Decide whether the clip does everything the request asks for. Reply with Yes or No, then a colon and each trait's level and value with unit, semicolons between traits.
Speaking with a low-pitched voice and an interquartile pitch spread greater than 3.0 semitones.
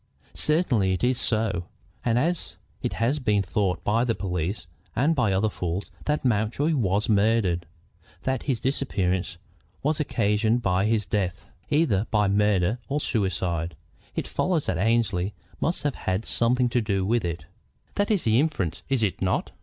Yes: low, 110 Hz; average, 5.0 semitones